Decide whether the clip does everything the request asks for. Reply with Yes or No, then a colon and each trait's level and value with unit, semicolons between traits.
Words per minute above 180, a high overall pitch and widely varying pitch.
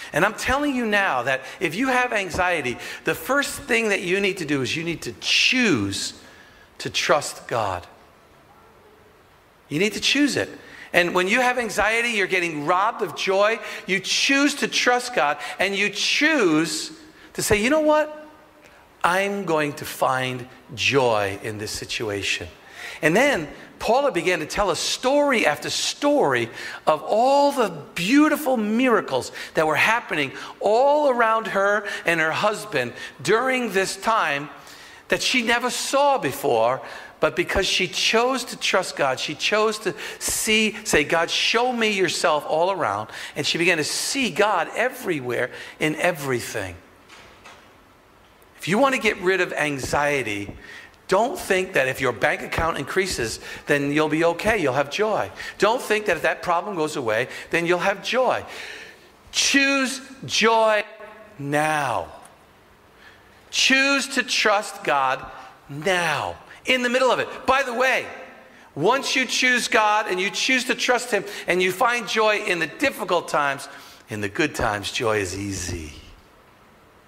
No: average, 155 wpm; high, 205 Hz; wide, 8.2 semitones